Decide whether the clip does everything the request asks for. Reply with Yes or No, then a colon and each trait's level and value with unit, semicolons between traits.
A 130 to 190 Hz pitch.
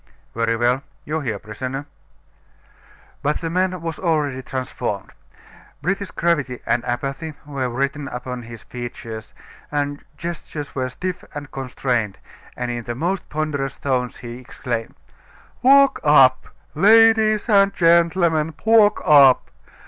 Yes: medium, 140 Hz